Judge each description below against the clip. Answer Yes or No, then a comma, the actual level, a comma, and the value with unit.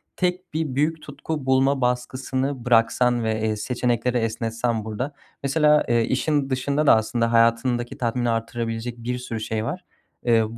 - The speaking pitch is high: No, low, 125 Hz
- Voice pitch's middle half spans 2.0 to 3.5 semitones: Yes, average, 3.0 semitones